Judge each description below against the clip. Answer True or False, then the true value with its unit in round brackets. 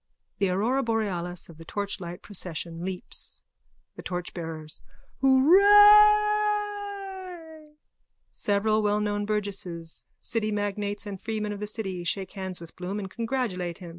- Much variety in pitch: True (6.8 semitones)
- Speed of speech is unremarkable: False (120 wpm)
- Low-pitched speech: False (205 Hz)